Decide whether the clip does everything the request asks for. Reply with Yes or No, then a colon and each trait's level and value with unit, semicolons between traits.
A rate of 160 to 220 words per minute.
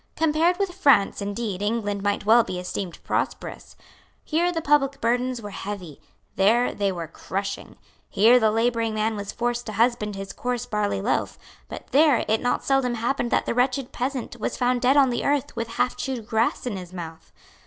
Yes: average, 185 wpm